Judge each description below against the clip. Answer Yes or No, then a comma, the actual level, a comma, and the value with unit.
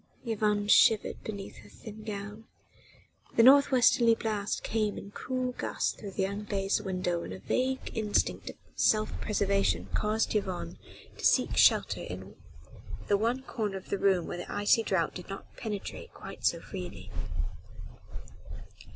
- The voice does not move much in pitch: Yes, narrow, 2.3 semitones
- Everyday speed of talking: Yes, average, 150 wpm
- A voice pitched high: Yes, high, 205 Hz